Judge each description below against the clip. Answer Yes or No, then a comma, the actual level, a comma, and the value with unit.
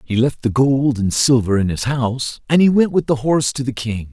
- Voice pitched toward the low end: Yes, low, 125 Hz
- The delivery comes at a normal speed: No, fast, 260 wpm